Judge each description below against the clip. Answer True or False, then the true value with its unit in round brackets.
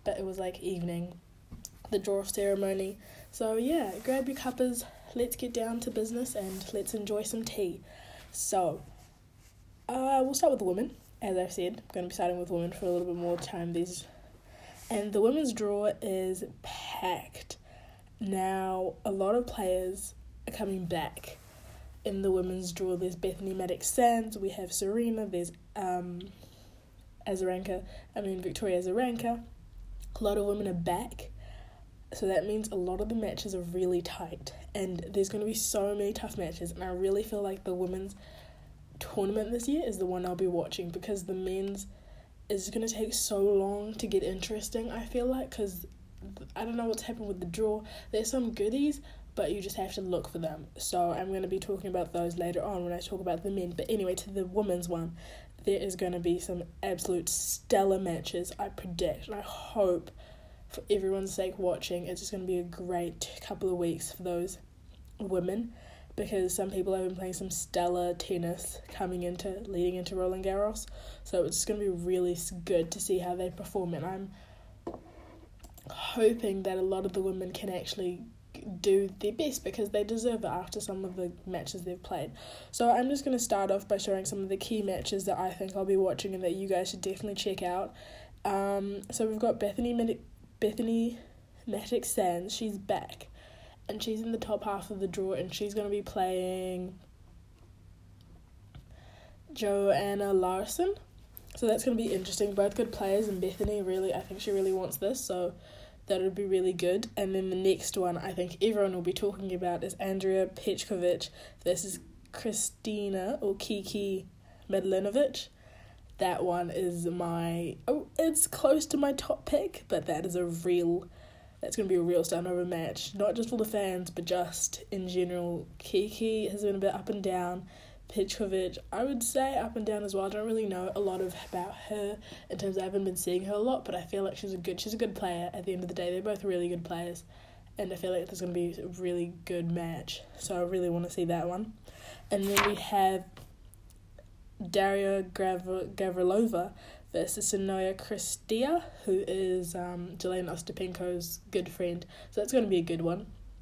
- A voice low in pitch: False (190 Hz)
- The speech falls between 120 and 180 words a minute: False (195 wpm)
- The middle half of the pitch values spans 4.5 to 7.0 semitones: False (2.7 semitones)